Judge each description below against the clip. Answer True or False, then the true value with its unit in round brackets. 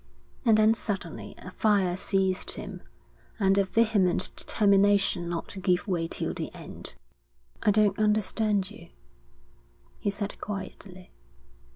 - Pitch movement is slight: True (2.2 semitones)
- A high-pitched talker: True (200 Hz)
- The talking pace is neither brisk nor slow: False (130 wpm)